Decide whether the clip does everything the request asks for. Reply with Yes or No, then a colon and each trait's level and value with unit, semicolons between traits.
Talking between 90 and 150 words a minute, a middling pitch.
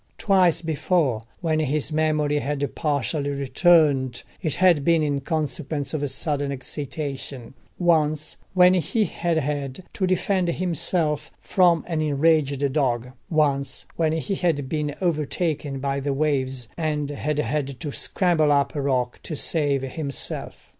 Yes: average, 140 wpm; medium, 150 Hz